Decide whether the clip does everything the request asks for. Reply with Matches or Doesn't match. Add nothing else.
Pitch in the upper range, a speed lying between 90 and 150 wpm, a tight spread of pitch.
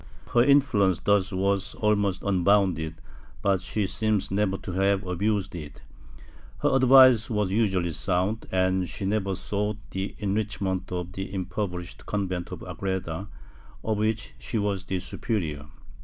Doesn't match